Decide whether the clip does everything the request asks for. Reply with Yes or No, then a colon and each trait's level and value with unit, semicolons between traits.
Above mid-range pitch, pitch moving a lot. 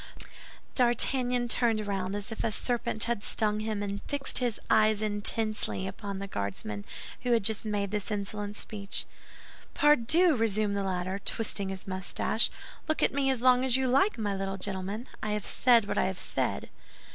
No: high, 215 Hz; average, 3.3 semitones